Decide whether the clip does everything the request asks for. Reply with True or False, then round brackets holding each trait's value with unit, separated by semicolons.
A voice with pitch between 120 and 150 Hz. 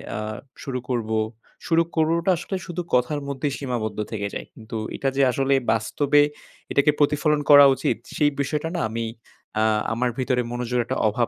True (135 Hz)